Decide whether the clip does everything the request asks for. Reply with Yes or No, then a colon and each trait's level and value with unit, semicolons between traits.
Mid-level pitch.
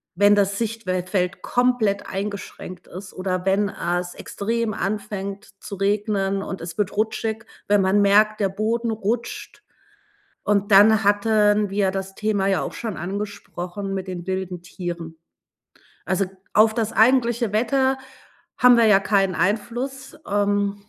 No: high, 205 Hz